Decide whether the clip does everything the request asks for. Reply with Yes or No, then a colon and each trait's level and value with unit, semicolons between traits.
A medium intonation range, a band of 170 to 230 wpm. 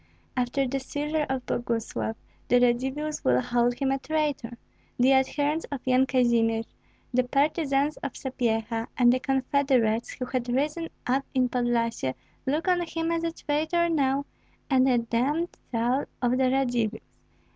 No: average, 3.1 semitones; average, 150 wpm